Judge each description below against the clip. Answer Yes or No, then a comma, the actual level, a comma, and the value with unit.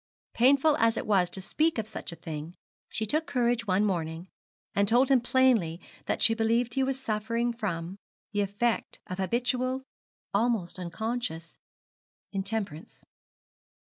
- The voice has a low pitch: No, high, 220 Hz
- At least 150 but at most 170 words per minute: No, average, 140 wpm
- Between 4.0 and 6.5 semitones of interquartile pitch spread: Yes, average, 4.6 semitones